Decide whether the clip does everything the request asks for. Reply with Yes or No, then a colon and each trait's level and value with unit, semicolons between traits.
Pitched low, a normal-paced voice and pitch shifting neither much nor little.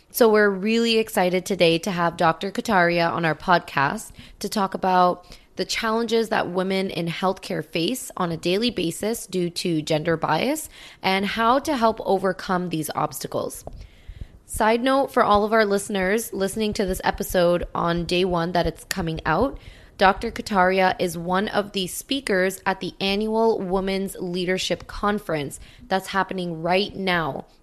No: medium, 185 Hz; average, 155 wpm; average, 3.3 semitones